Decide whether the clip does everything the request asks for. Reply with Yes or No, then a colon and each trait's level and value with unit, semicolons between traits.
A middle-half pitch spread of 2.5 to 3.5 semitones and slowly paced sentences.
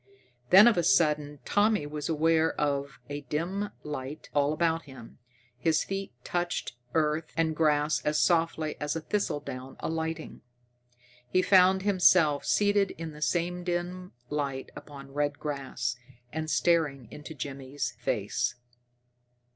Yes: average, 3.2 semitones; slow, 130 wpm